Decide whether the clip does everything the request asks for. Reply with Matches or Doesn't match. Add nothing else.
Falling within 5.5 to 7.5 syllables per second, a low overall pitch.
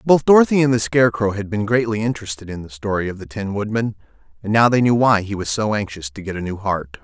Matches